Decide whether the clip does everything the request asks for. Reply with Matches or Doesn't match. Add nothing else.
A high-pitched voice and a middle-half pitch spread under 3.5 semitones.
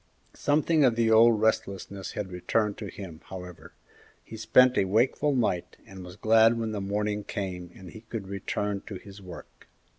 Doesn't match